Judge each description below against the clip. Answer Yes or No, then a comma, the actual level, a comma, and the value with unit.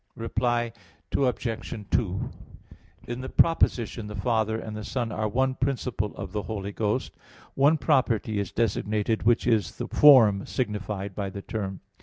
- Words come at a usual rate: Yes, average, 150 wpm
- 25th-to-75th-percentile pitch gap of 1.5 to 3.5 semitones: Yes, average, 3.0 semitones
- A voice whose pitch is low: Yes, low, 110 Hz